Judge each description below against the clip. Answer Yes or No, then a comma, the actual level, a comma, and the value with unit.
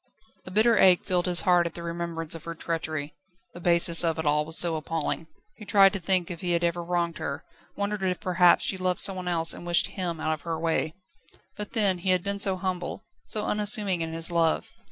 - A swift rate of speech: Yes, fast, 225 wpm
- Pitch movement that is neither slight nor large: No, narrow, 2.2 semitones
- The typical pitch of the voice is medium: Yes, medium, 175 Hz